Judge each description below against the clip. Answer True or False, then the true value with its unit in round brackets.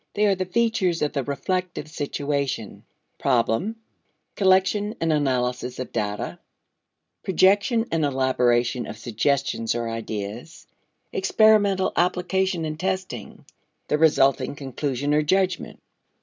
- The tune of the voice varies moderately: False (7.0 semitones)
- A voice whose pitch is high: False (150 Hz)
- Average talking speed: False (110 wpm)